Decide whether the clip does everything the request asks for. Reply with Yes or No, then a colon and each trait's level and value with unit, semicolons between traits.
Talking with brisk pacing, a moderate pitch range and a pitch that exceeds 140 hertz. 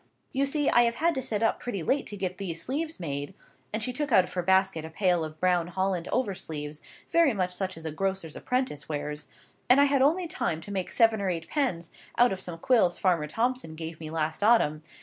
No: fast, 225 wpm; wide, 7.0 semitones; high, 190 Hz